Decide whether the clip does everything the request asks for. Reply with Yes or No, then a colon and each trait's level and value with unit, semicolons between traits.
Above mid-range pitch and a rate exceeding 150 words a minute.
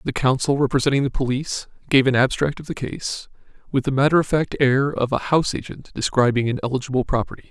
No: low, 135 Hz; average, 200 wpm